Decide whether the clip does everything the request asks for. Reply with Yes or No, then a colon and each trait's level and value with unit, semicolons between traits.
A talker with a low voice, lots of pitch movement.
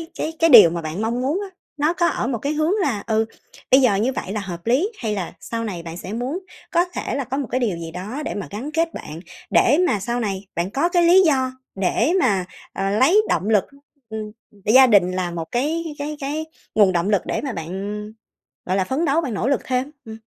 No: high, 230 Hz; wide, 6.6 semitones